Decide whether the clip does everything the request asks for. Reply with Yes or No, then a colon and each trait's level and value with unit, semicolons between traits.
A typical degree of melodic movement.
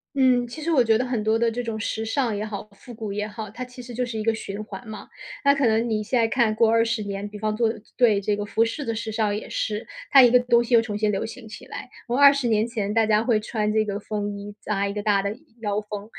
No: narrow, 2.2 semitones